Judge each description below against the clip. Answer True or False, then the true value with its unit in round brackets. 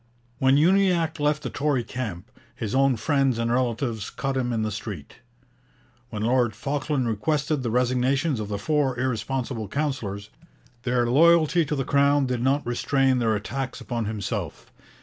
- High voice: False (130 Hz)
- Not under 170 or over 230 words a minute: False (155 wpm)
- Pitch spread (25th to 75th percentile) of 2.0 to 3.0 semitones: False (3.7 semitones)